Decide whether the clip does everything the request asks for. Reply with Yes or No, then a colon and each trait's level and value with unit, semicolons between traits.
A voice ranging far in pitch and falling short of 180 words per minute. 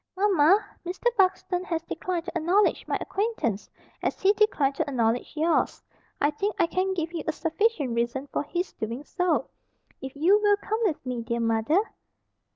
Yes: wide, 6.1 semitones; average, 170 wpm